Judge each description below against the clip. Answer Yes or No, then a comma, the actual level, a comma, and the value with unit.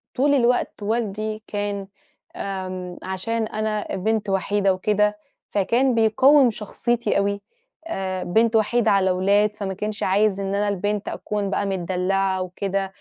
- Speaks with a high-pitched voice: Yes, high, 205 Hz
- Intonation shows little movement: Yes, narrow, 2.1 semitones